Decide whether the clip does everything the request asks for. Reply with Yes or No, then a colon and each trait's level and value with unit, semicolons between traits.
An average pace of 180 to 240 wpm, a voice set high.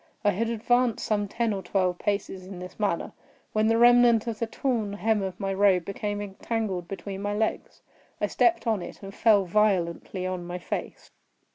Yes: average, 185 wpm; high, 205 Hz